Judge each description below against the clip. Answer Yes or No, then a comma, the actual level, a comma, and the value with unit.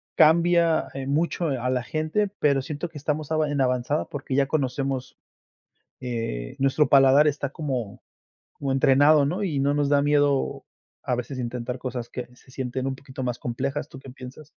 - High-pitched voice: No, low, 135 Hz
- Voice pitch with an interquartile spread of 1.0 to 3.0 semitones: Yes, narrow, 2.5 semitones